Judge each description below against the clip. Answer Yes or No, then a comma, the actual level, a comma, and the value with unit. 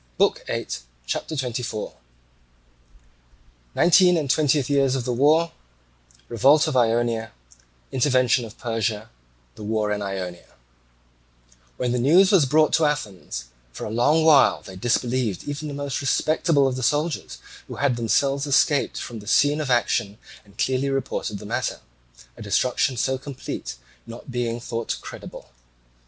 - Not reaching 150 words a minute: Yes, average, 140 wpm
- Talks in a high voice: No, low, 125 Hz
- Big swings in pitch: No, average, 4.6 semitones